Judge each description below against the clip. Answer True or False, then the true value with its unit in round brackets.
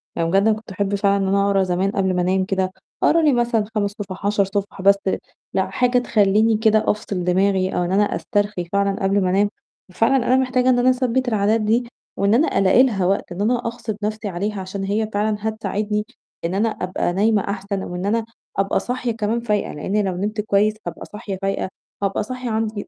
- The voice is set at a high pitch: True (205 Hz)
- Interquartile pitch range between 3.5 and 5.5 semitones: False (2.4 semitones)